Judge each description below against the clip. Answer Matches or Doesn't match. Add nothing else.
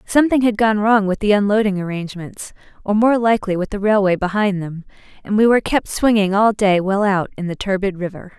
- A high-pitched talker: Matches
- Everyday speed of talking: Doesn't match